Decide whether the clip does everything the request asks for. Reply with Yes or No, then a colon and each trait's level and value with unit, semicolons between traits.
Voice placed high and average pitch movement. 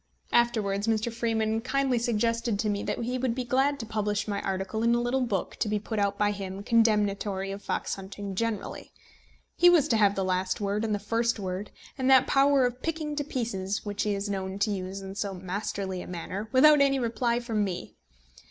Yes: high, 215 Hz; average, 3.2 semitones